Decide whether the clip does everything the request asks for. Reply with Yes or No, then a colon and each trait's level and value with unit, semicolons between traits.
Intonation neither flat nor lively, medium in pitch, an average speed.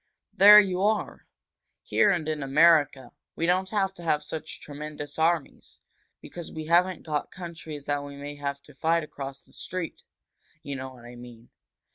Yes: average, 3.5 semitones; medium, 155 Hz; average, 170 wpm